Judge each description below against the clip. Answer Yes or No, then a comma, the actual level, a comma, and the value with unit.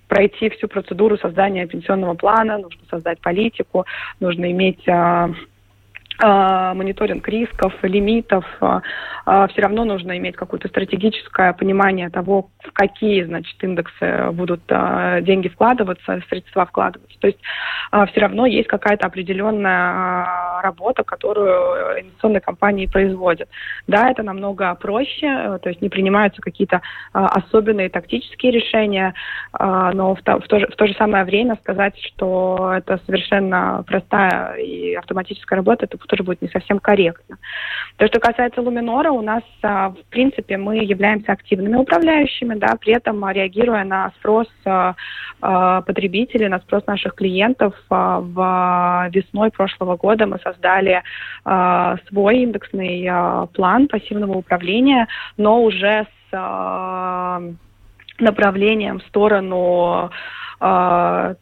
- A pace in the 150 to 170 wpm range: No, average, 125 wpm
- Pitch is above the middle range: Yes, high, 195 Hz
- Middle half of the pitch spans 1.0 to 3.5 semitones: Yes, average, 2.9 semitones